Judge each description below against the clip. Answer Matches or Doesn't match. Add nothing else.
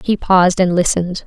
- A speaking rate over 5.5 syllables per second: Matches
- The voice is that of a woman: Matches